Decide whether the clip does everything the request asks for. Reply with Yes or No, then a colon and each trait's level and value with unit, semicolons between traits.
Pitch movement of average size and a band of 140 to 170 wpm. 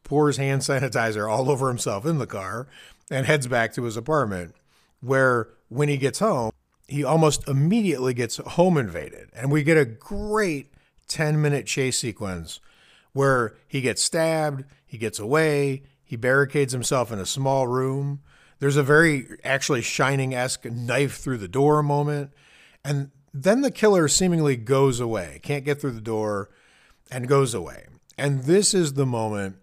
Yes: average, 3.3 semitones; average, 160 wpm